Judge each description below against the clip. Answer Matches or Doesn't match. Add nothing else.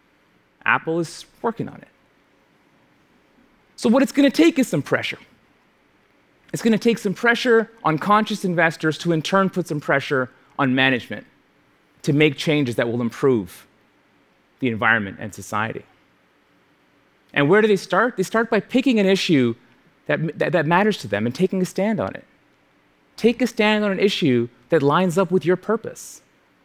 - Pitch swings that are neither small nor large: Doesn't match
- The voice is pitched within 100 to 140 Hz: Doesn't match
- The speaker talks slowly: Doesn't match